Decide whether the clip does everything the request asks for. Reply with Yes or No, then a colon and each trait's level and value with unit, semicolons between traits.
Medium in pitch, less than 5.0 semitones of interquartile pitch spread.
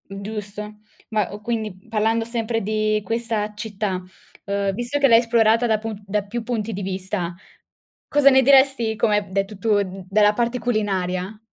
No: high, 215 Hz; narrow, 2.4 semitones